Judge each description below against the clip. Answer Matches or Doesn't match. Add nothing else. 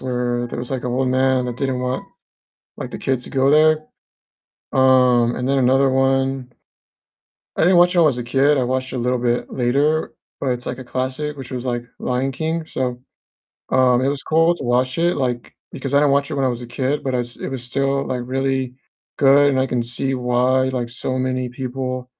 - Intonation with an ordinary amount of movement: Doesn't match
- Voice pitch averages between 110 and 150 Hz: Matches